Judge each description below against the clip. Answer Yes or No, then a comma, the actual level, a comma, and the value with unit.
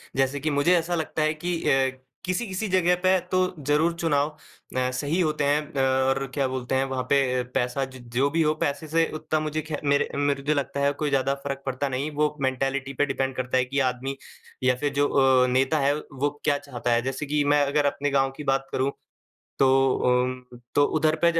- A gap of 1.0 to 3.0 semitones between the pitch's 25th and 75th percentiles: Yes, narrow, 2.4 semitones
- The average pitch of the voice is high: No, medium, 140 Hz